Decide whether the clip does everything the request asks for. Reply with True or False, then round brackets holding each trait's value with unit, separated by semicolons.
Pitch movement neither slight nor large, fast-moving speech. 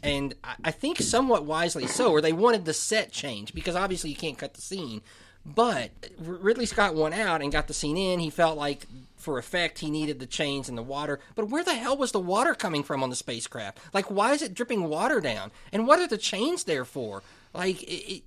False (7.3 semitones; 230 wpm)